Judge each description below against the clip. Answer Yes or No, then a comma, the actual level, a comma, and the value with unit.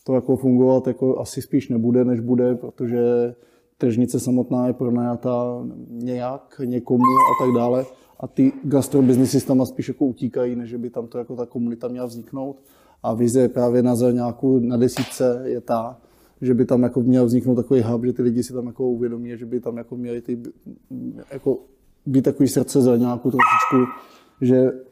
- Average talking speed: No, fast, 175 wpm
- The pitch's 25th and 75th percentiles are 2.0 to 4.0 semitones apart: No, narrow, 1.2 semitones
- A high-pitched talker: No, low, 125 Hz